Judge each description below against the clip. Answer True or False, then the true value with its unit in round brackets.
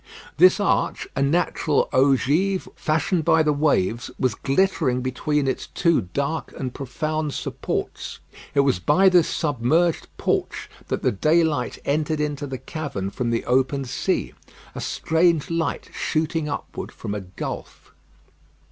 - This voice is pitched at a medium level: True (145 Hz)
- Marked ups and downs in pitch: False (3.8 semitones)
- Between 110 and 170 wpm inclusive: True (140 wpm)